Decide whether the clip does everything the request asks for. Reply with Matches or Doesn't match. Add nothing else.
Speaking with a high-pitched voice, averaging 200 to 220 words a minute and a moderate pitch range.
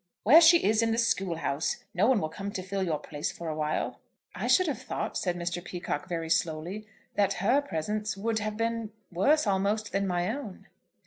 Matches